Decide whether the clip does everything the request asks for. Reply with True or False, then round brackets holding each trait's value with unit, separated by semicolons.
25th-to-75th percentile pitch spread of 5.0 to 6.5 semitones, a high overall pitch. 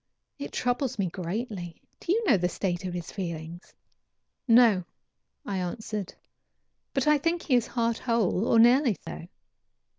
True (5.6 semitones; 220 Hz)